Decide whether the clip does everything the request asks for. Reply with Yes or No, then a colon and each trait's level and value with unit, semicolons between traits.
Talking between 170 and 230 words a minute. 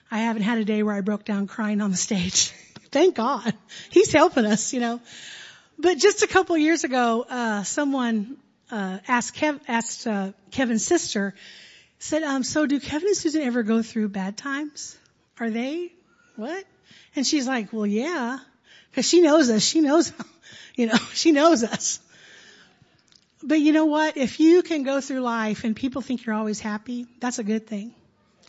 Yes: average, 185 wpm